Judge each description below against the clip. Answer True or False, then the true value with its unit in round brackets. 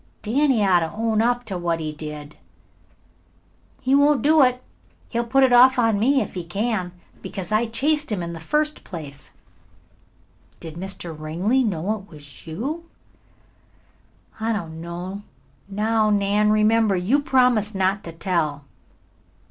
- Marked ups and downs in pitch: True (6.1 semitones)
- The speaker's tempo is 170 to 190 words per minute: False (150 wpm)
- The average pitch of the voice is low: False (210 Hz)